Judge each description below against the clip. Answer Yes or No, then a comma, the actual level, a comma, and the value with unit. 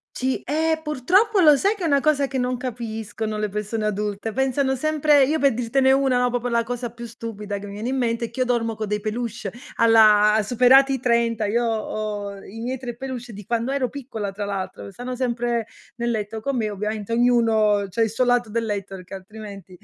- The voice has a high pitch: Yes, high, 235 Hz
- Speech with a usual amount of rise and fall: Yes, average, 3.2 semitones